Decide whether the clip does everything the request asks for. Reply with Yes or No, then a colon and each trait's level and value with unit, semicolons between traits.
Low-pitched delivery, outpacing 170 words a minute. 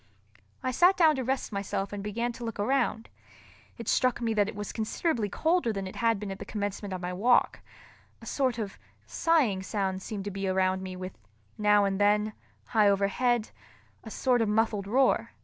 No: high, 210 Hz; average, 190 wpm